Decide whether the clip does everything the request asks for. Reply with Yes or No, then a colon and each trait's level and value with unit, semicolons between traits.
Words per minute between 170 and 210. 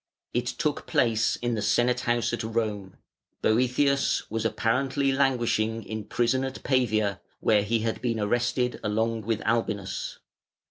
No: average, 140 wpm